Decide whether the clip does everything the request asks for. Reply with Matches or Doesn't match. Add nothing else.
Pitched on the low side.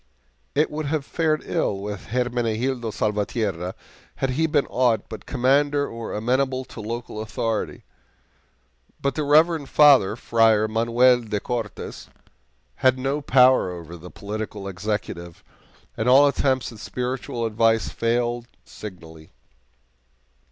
Matches